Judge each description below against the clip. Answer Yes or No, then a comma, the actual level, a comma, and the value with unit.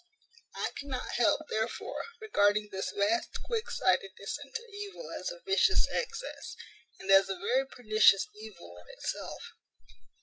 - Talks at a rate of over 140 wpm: No, slow, 135 wpm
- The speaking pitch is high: Yes, high, 220 Hz